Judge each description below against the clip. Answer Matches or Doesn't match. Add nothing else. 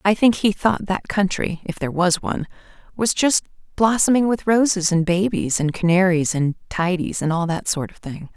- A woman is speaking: Matches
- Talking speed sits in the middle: Matches